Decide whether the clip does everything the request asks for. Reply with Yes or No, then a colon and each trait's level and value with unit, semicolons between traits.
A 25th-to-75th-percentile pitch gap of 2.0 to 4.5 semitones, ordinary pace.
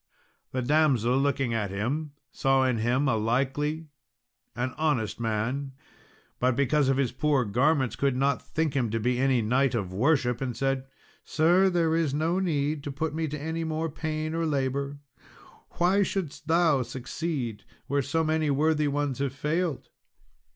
Yes: average, 3.6 semitones; average, 165 wpm